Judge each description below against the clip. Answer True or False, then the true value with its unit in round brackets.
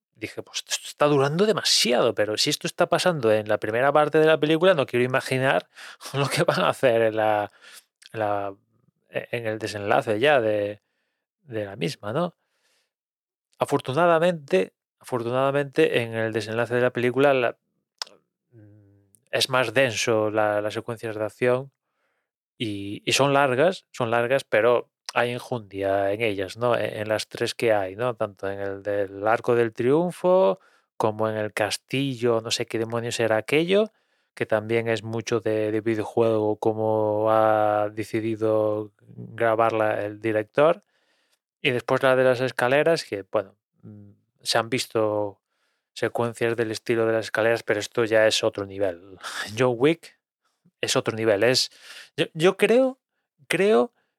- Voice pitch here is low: True (115 Hz)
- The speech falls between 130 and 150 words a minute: True (145 wpm)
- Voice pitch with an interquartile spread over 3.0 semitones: True (3.6 semitones)